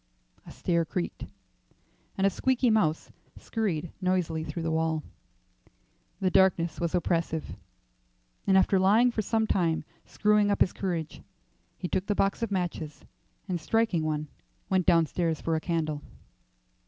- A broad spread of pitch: No, average, 3.5 semitones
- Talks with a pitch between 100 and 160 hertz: No, medium, 175 Hz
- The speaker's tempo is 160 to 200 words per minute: No, average, 140 wpm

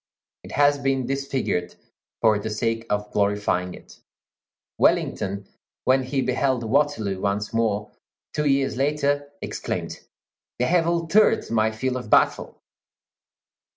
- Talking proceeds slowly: Yes, slow, 120 wpm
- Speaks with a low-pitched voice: Yes, low, 125 Hz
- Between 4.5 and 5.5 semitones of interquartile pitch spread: Yes, average, 5.1 semitones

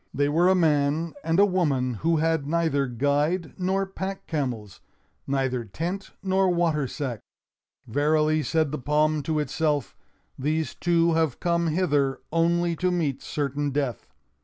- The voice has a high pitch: No, medium, 155 Hz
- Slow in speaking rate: No, average, 145 wpm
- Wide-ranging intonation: No, average, 3.1 semitones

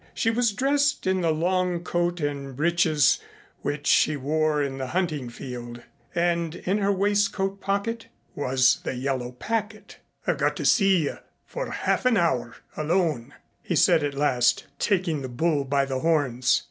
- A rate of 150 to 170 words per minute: Yes, average, 160 wpm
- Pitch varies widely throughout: Yes, wide, 5.9 semitones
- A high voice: No, medium, 160 Hz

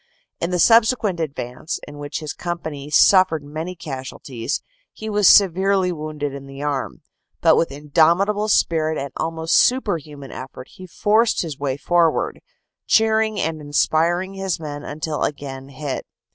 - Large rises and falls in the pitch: No, average, 4.4 semitones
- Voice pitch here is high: No, medium, 160 Hz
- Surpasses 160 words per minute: No, average, 145 wpm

